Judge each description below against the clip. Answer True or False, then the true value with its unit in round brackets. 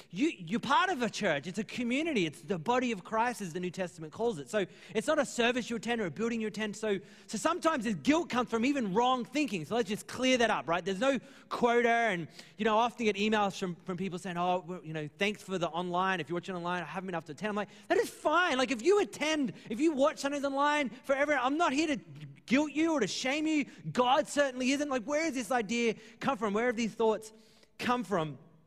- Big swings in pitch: True (5.9 semitones)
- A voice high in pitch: True (225 Hz)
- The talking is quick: True (255 wpm)